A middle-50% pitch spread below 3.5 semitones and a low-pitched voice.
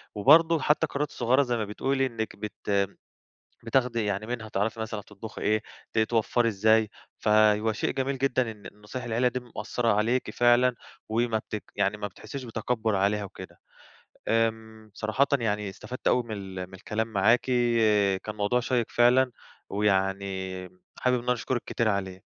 Yes: average, 2.8 semitones; low, 110 Hz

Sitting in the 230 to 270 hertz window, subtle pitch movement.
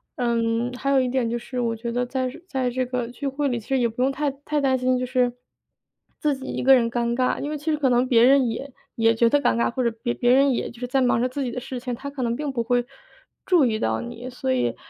Yes: very high, 250 Hz; narrow, 2.2 semitones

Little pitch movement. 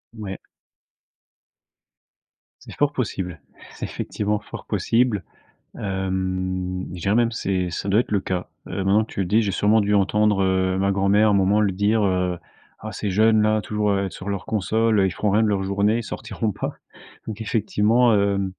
Yes: narrow, 2.1 semitones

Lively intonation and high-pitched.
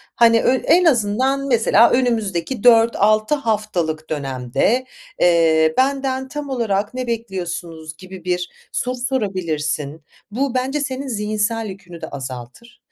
Yes: wide, 6.8 semitones; high, 215 Hz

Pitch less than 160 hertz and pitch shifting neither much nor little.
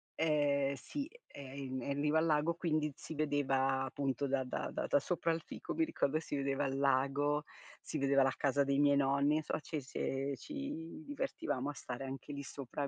No: medium, 140 Hz; narrow, 2.1 semitones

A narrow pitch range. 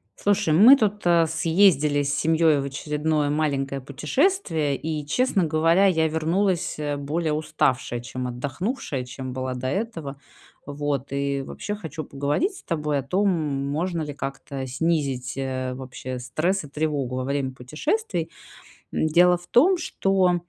No: average, 4.2 semitones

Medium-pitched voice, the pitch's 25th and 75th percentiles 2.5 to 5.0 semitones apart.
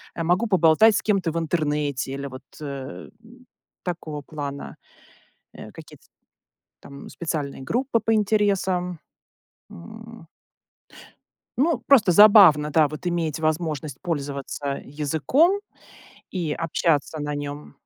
No: medium, 165 Hz; wide, 5.6 semitones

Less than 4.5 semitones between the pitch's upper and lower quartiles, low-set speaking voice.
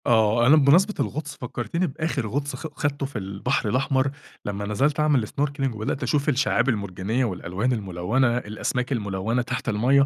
No: average, 4.8 semitones; low, 125 Hz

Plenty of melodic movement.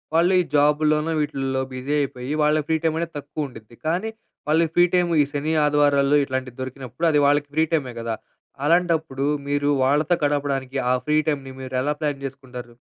No: average, 2.8 semitones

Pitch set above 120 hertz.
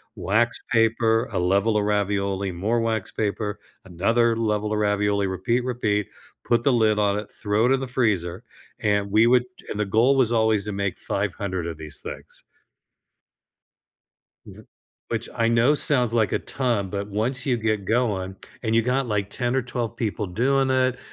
No: low, 110 Hz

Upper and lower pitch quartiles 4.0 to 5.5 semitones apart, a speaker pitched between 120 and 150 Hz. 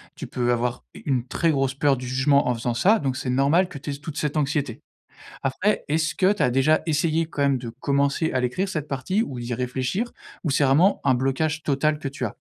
No: average, 3.3 semitones; medium, 140 Hz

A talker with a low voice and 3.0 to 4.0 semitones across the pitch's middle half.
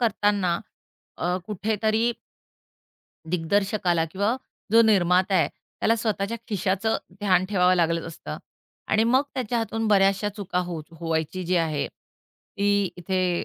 No: high, 195 Hz; average, 3.5 semitones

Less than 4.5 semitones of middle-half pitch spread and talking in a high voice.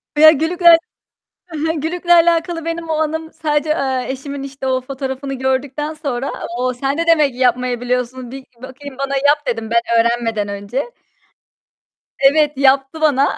Yes: average, 3.4 semitones; very high, 275 Hz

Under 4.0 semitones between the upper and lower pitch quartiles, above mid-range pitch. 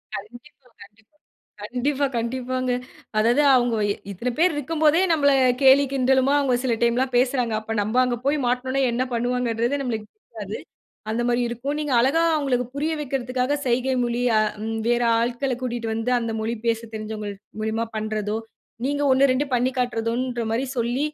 Yes: narrow, 2.5 semitones; high, 245 Hz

